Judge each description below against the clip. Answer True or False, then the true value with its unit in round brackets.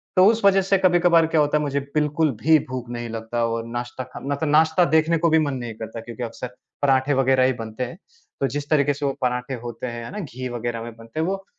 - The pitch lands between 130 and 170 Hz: True (135 Hz)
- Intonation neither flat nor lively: True (4.8 semitones)